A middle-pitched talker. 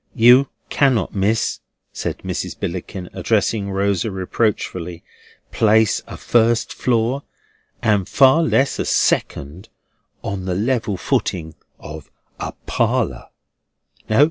No: low, 105 Hz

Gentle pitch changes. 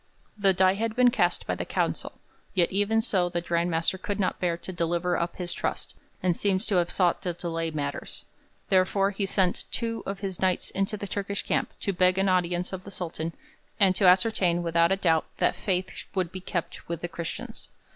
Yes: narrow, 2.3 semitones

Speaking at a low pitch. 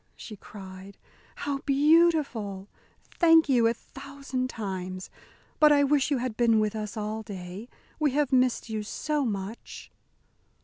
No: high, 235 Hz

